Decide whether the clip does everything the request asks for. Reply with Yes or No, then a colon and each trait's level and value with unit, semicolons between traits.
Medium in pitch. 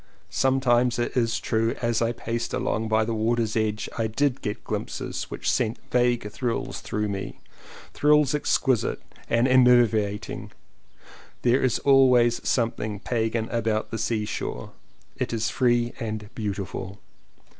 No: low, 115 Hz